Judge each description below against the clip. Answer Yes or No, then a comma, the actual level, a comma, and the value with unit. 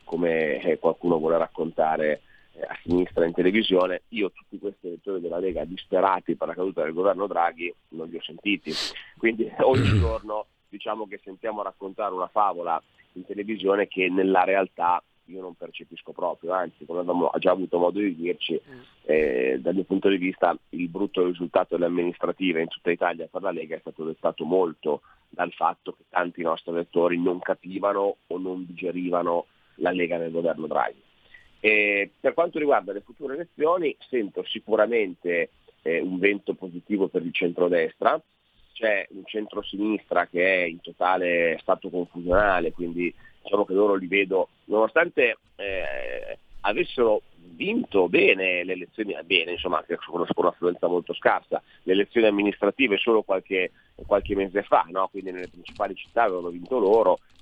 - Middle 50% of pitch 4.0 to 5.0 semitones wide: No, average, 2.8 semitones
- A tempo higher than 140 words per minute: Yes, average, 155 wpm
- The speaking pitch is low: Yes, very low, 95 Hz